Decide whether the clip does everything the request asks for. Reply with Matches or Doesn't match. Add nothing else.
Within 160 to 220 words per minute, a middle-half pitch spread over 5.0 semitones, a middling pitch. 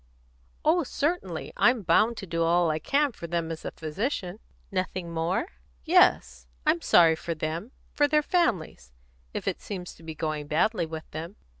Matches